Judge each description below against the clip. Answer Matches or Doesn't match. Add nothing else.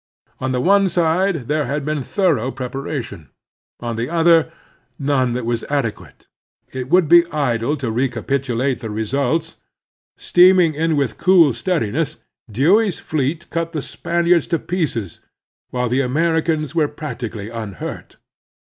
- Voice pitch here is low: Doesn't match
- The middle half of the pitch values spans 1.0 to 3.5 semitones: Doesn't match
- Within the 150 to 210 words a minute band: Doesn't match